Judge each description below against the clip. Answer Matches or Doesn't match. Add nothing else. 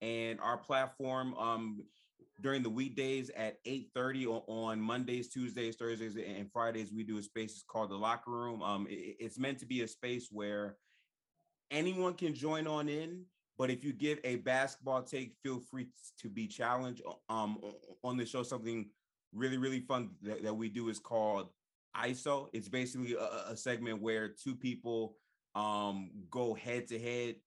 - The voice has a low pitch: Matches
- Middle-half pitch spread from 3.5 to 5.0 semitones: Doesn't match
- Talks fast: Doesn't match